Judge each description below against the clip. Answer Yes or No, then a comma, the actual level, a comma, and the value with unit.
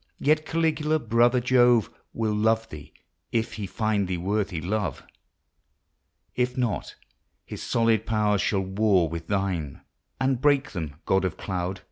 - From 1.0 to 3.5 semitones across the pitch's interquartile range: No, average, 4.4 semitones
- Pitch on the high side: No, low, 110 Hz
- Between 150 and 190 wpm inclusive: No, average, 140 wpm